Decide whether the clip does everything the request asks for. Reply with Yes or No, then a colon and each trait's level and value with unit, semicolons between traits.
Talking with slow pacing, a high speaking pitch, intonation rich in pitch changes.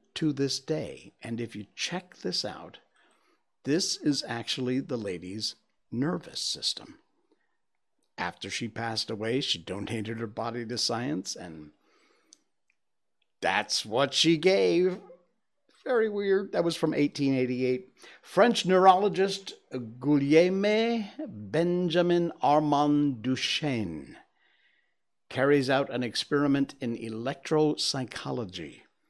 No: slow, 100 wpm; medium, 140 Hz; wide, 6.7 semitones